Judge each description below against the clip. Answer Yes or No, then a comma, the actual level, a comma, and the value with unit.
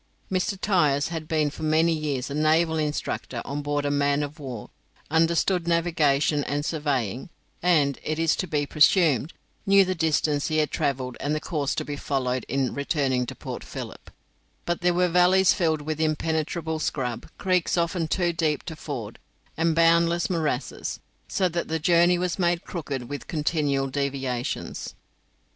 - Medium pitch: Yes, medium, 155 Hz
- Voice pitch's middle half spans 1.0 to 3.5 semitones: Yes, average, 2.9 semitones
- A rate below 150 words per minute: No, average, 165 wpm